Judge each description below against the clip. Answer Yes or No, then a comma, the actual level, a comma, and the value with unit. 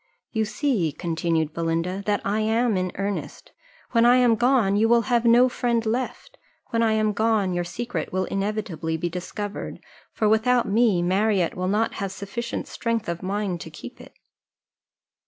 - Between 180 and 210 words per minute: No, average, 170 wpm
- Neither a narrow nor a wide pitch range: Yes, average, 4.1 semitones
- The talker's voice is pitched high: Yes, high, 210 Hz